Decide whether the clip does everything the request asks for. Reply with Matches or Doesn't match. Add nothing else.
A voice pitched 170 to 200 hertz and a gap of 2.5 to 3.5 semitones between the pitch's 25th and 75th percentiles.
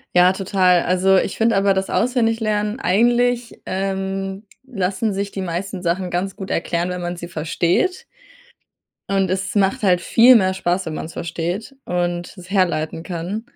Matches